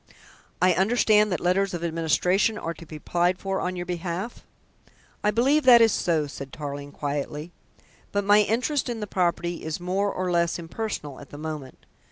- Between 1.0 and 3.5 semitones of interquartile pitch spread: No, average, 4.4 semitones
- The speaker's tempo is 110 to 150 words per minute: No, average, 180 wpm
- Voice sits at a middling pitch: Yes, medium, 180 Hz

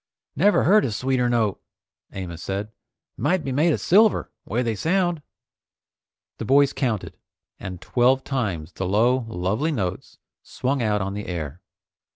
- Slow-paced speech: No, average, 150 wpm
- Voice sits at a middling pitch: No, low, 120 Hz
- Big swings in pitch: Yes, wide, 6.3 semitones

